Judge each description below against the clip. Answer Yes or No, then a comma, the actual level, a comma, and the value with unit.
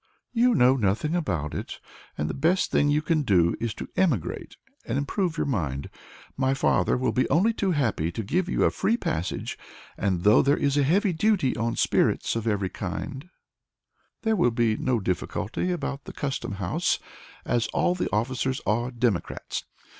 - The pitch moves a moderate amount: No, wide, 7.5 semitones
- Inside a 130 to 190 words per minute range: Yes, average, 175 wpm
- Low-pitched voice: Yes, low, 130 Hz